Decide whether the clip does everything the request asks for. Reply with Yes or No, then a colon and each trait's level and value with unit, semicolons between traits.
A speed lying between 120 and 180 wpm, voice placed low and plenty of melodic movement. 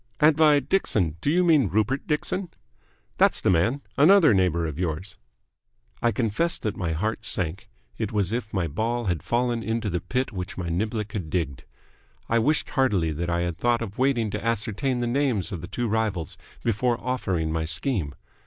No: average, 190 wpm; low, 110 Hz; wide, 6.1 semitones